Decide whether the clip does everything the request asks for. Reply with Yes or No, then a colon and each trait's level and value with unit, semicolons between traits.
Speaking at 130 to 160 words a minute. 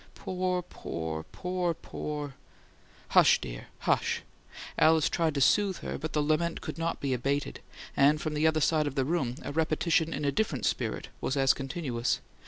No: average, 180 wpm